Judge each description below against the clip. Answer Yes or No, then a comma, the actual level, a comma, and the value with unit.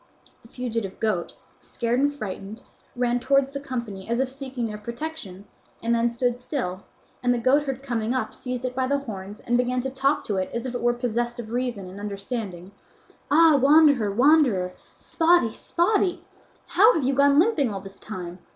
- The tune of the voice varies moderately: Yes, average, 4.2 semitones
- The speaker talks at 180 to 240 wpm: Yes, average, 185 wpm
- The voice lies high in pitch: Yes, high, 245 Hz